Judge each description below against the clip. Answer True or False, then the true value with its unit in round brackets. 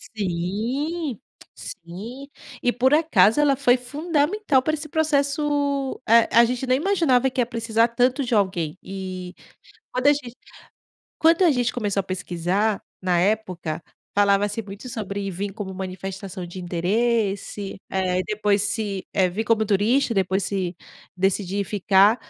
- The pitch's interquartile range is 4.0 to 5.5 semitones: True (5.2 semitones)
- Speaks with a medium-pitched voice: False (215 Hz)